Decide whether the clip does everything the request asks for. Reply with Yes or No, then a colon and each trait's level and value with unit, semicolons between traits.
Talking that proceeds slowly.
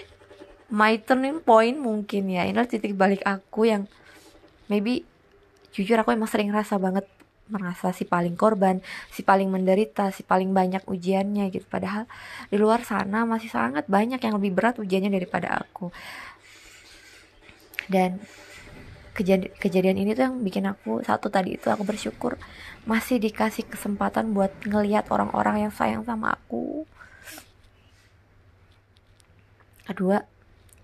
No: average, 130 wpm